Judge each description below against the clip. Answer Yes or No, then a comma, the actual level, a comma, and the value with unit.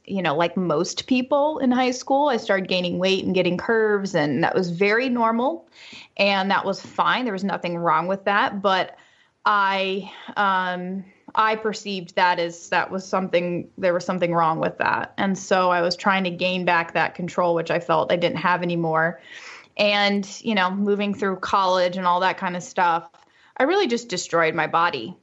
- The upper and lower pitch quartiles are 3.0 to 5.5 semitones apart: No, narrow, 2.6 semitones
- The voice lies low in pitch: No, high, 190 Hz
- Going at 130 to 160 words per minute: No, average, 195 wpm